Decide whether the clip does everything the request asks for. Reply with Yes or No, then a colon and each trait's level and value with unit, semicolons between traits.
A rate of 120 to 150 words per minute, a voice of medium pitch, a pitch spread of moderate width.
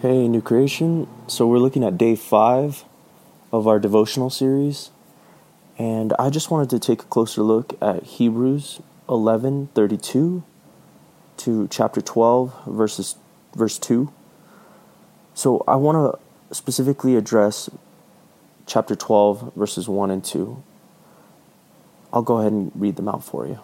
No: slow, 135 wpm; low, 120 Hz; average, 3.9 semitones